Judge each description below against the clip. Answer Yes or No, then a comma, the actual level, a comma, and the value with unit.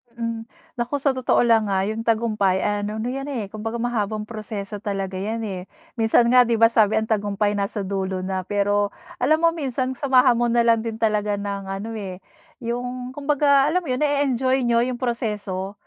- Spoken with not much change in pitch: No, average, 3.4 semitones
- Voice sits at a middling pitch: No, high, 225 Hz